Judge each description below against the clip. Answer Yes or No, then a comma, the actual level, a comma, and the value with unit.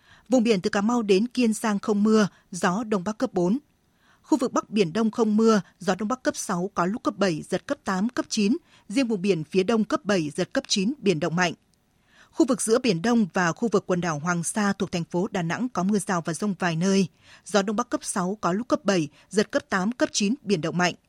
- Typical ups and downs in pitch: Yes, average, 4.2 semitones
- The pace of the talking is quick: Yes, fast, 255 wpm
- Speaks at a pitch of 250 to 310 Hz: No, high, 205 Hz